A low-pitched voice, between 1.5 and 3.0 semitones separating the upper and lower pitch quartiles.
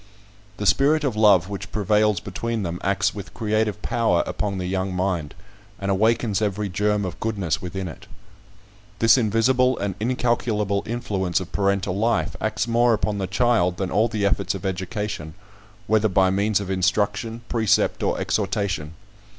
Yes: low, 100 Hz; average, 2.7 semitones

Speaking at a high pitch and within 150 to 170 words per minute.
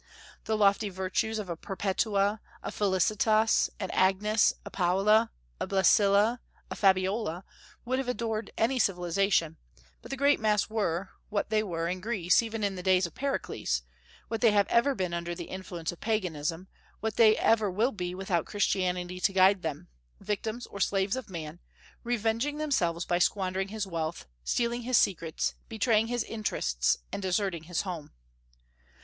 Yes: high, 200 Hz; average, 160 wpm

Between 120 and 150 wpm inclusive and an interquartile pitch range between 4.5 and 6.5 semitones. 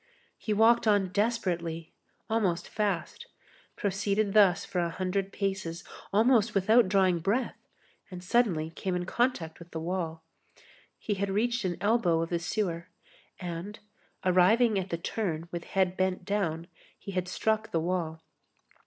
No: average, 145 wpm; average, 3.5 semitones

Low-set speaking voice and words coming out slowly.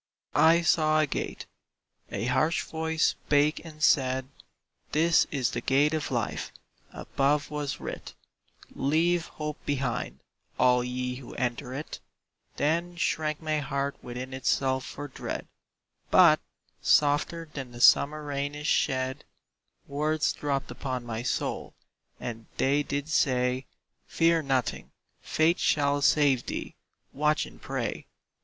No: medium, 145 Hz; slow, 130 wpm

